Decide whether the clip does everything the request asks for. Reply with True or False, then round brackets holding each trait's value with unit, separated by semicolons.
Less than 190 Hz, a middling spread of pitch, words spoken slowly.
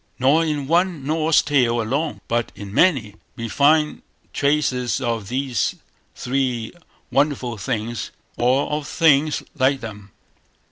True (135 Hz; 4.2 semitones; 125 wpm)